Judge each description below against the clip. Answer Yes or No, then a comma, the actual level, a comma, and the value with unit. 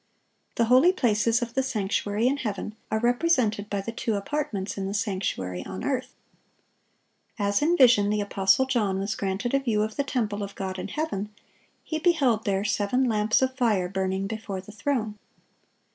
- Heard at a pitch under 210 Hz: No, high, 215 Hz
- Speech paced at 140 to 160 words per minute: No, average, 175 wpm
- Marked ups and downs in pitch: No, average, 4.1 semitones